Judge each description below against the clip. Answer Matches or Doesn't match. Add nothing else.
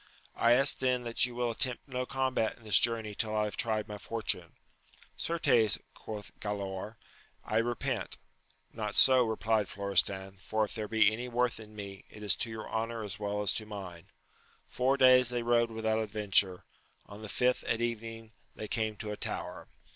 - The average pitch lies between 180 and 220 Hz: Doesn't match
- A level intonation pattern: Matches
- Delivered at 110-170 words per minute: Doesn't match